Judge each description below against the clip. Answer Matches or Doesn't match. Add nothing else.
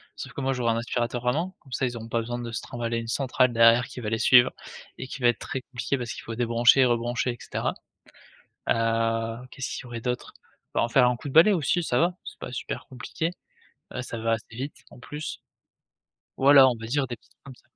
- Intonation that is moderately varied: Doesn't match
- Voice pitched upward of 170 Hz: Doesn't match